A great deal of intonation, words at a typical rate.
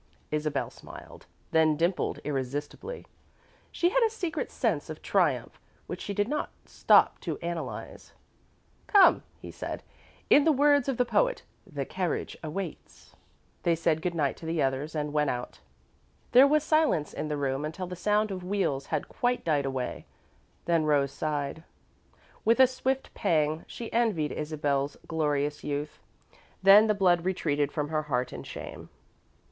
Yes: wide, 6.4 semitones; average, 155 wpm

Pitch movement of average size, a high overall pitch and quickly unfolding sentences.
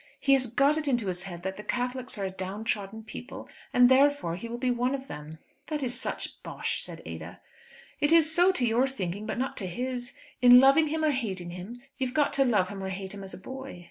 No: wide, 5.7 semitones; high, 245 Hz; fast, 235 wpm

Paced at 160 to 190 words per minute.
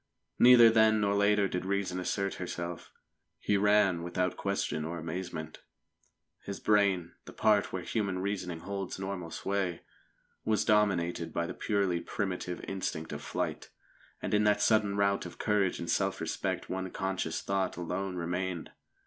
No: average, 150 wpm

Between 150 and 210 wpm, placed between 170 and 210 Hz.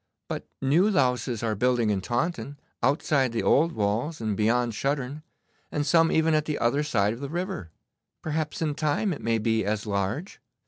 No: average, 180 wpm; low, 135 Hz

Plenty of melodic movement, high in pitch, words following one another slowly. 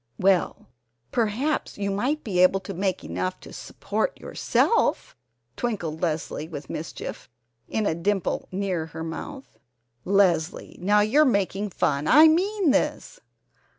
Yes: wide, 6.4 semitones; high, 195 Hz; slow, 130 wpm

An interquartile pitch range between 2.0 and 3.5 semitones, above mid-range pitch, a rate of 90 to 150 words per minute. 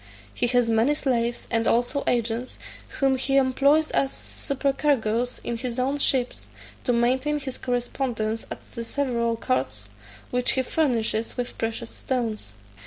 Yes: average, 2.7 semitones; high, 245 Hz; average, 140 wpm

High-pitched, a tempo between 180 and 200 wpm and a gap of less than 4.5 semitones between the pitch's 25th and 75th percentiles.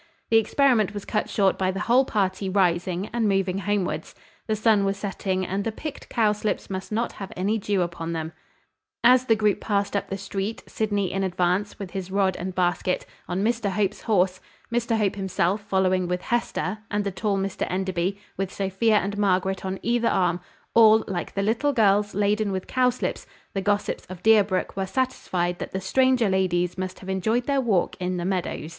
Yes: high, 195 Hz; average, 190 wpm; narrow, 2.5 semitones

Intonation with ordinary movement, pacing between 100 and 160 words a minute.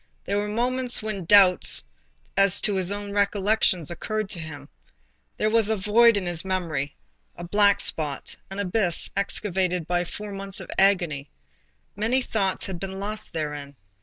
Yes: average, 3.2 semitones; average, 155 wpm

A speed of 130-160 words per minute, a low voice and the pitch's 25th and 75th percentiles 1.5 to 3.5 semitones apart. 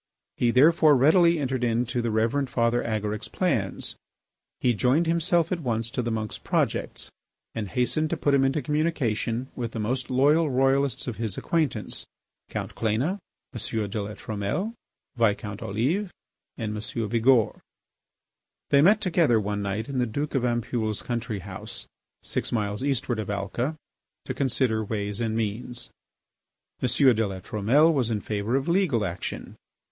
No: average, 155 wpm; low, 120 Hz; average, 4.3 semitones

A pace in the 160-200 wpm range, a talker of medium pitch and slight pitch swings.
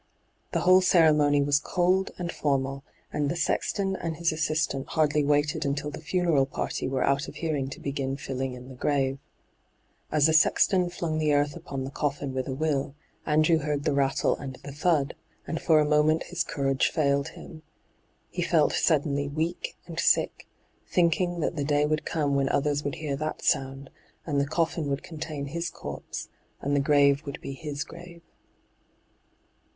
Yes: average, 175 wpm; medium, 150 Hz; narrow, 2.3 semitones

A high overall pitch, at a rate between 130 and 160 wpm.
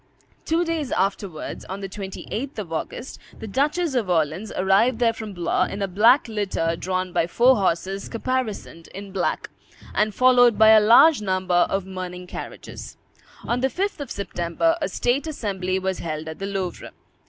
No: high, 200 Hz; average, 170 wpm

